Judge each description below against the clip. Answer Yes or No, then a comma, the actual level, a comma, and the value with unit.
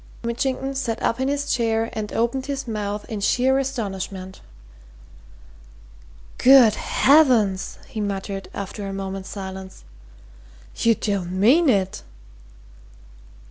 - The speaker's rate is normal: No, slow, 110 wpm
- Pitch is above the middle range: Yes, high, 220 Hz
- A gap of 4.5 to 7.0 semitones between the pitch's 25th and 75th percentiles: Yes, average, 5.0 semitones